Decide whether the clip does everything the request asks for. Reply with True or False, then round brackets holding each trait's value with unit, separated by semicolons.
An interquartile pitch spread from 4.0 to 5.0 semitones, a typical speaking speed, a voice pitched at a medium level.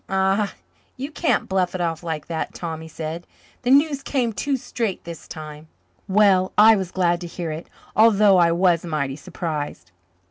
True (4.5 semitones; 175 wpm; 180 Hz)